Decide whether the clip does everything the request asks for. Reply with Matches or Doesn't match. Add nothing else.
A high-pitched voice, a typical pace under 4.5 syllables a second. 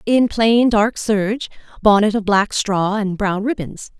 Matches